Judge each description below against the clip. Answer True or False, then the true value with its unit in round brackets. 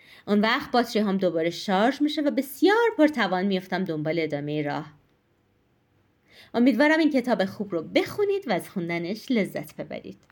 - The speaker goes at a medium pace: True (145 wpm)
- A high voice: True (205 Hz)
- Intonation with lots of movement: True (8.1 semitones)